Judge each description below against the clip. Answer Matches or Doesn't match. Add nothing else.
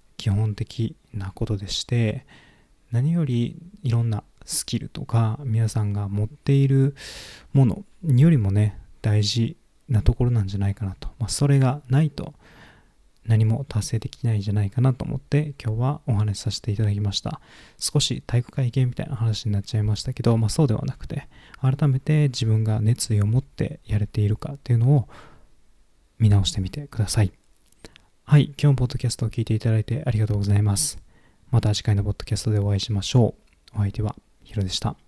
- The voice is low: Matches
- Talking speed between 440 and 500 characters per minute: Doesn't match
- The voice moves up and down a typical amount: Matches